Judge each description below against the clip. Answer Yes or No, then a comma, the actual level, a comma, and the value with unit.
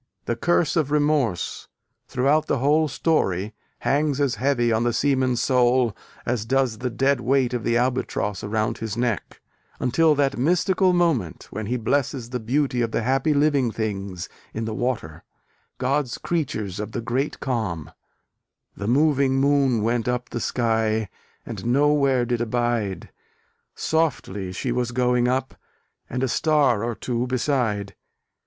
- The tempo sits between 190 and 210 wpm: No, average, 150 wpm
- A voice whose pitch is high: No, low, 125 Hz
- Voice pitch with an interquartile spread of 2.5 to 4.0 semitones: Yes, average, 3.7 semitones